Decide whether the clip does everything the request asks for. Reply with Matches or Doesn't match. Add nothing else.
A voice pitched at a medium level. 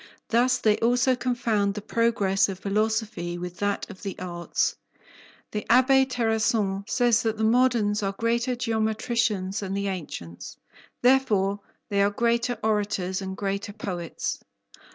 Doesn't match